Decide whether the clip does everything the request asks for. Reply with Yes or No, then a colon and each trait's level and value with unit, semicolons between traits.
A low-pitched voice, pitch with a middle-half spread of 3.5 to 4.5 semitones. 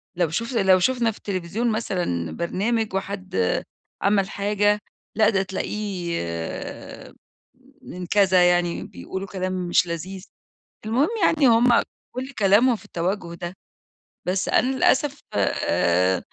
No: high, 195 Hz; average, 3.8 semitones